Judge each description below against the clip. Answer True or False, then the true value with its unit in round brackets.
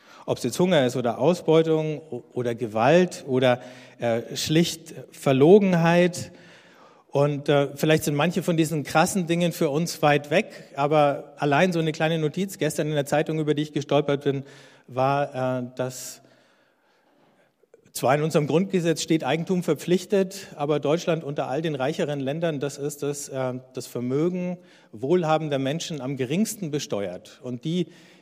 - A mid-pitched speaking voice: True (150 Hz)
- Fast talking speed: False (150 wpm)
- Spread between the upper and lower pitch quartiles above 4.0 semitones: False (3.5 semitones)